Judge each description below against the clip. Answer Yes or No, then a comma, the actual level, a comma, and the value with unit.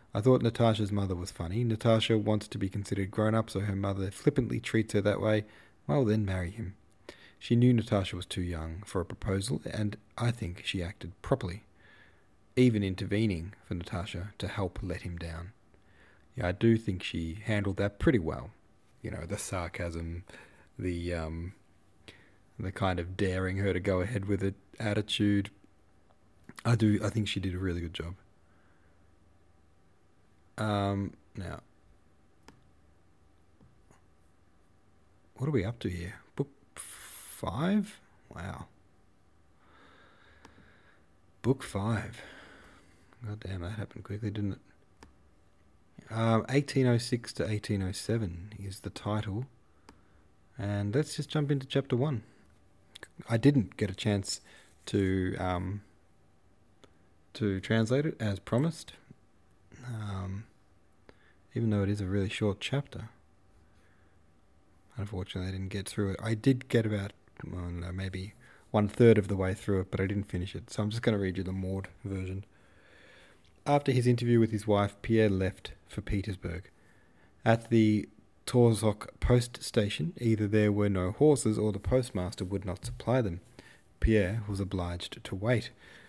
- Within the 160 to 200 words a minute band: No, average, 145 wpm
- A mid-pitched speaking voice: No, low, 100 Hz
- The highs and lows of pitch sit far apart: No, average, 3.5 semitones